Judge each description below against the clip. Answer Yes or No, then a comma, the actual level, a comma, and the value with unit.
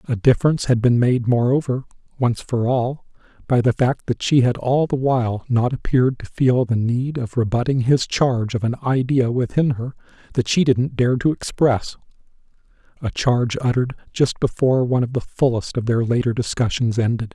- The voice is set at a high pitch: No, low, 125 Hz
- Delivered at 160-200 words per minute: Yes, average, 180 wpm